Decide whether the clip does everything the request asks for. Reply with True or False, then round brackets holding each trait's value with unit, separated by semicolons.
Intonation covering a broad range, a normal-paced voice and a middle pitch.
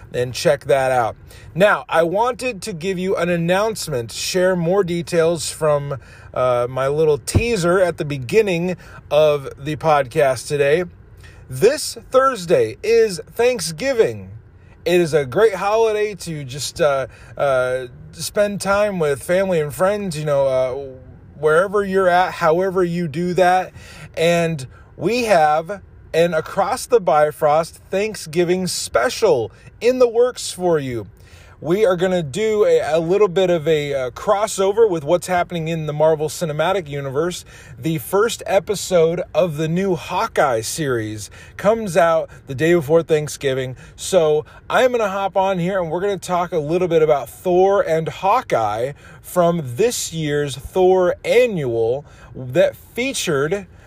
True (5.7 semitones; 145 wpm; 170 Hz)